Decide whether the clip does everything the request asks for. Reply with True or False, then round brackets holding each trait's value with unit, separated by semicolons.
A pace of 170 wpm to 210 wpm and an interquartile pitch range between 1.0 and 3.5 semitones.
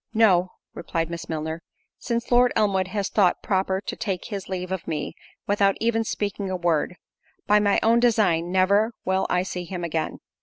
True (180 wpm; 3.0 semitones)